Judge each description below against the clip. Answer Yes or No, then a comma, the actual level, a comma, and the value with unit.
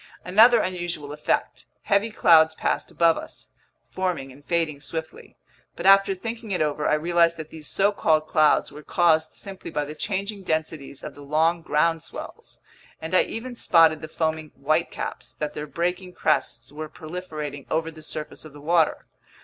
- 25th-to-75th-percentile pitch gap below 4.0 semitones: Yes, average, 3.0 semitones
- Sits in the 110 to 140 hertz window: No, medium, 160 Hz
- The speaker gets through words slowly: No, average, 175 wpm